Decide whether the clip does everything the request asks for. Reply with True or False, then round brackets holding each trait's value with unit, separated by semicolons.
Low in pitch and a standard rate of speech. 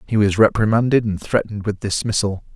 True (105 Hz; 165 wpm)